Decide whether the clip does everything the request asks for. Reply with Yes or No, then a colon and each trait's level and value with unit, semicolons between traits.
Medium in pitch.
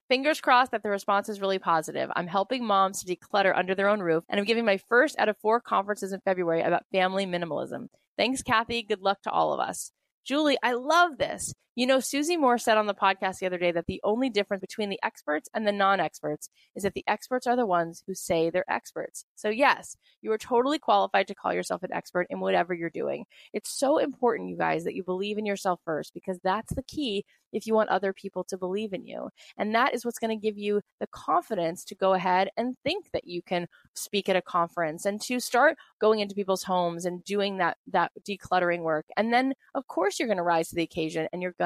No: high, 200 Hz